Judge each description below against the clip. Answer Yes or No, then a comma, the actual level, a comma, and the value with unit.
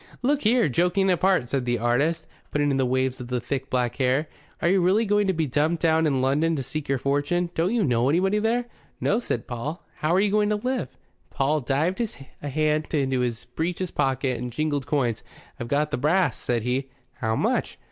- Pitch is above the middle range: No, medium, 150 Hz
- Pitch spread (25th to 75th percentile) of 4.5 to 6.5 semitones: Yes, wide, 5.6 semitones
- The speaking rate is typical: No, fast, 210 wpm